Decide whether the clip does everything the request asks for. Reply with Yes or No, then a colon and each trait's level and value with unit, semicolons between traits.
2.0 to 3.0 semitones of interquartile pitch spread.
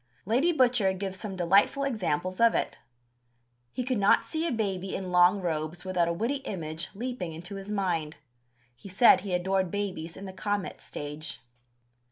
No: average, 3.4 semitones